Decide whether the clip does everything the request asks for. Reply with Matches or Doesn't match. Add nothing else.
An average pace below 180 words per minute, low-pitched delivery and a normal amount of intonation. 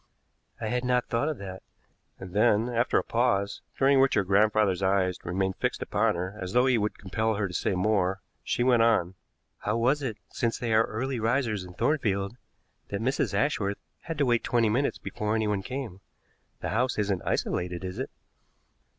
Doesn't match